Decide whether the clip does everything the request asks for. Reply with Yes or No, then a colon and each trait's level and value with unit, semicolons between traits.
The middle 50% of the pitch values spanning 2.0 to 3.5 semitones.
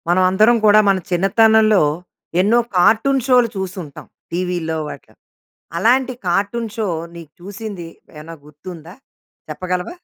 No: average, 4.2 semitones